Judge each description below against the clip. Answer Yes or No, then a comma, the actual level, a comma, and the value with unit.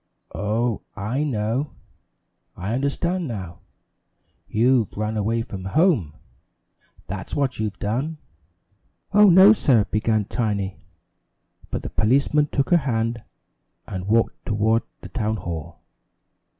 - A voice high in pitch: No, low, 115 Hz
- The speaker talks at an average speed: No, slow, 115 wpm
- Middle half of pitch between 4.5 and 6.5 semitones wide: Yes, average, 4.9 semitones